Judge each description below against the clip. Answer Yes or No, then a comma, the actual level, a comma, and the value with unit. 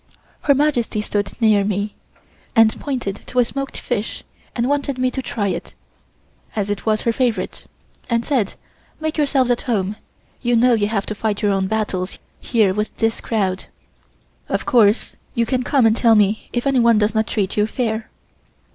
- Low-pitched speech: No, high, 225 Hz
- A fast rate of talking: No, average, 180 wpm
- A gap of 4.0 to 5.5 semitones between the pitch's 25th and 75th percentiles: No, average, 3.1 semitones